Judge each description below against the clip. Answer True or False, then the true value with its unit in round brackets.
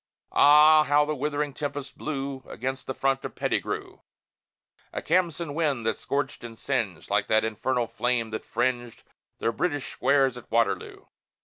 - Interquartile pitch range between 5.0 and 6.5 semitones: False (3.8 semitones)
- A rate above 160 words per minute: False (150 wpm)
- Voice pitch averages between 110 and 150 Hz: True (135 Hz)